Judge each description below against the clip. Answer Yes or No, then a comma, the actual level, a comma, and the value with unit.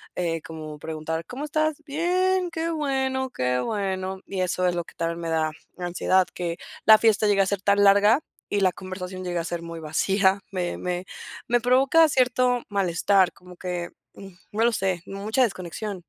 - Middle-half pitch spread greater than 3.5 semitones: Yes, wide, 5.6 semitones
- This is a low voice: No, high, 190 Hz